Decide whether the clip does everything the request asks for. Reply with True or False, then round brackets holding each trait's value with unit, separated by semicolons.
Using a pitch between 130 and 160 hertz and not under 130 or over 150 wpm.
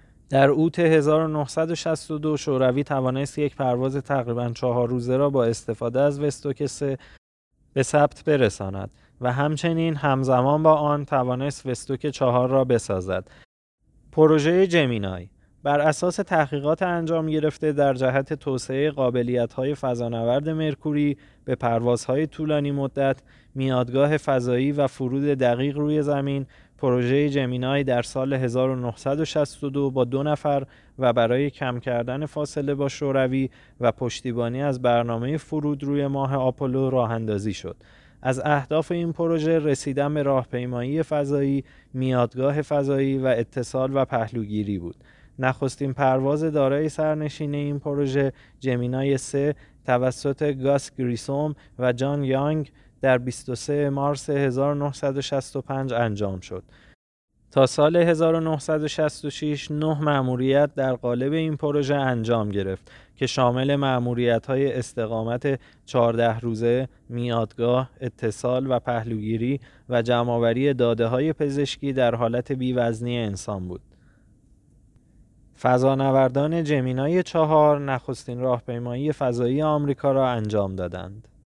False (135 Hz; 115 wpm)